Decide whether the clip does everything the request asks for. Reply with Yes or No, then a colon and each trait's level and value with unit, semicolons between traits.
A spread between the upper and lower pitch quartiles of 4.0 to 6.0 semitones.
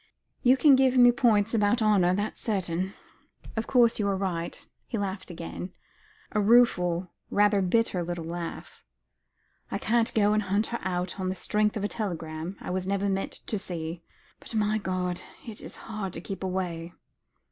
No: average, 3.3 semitones